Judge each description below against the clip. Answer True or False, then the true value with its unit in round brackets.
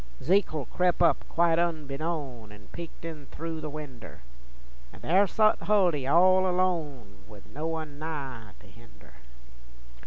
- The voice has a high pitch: False (155 Hz)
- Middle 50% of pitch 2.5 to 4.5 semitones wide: True (4.0 semitones)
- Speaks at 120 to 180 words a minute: True (135 wpm)